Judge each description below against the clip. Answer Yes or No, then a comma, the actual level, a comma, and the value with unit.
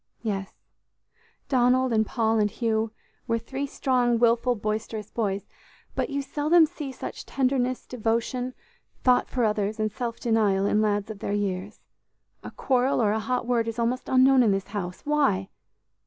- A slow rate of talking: No, average, 160 wpm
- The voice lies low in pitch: No, high, 230 Hz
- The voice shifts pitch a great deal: No, average, 3.2 semitones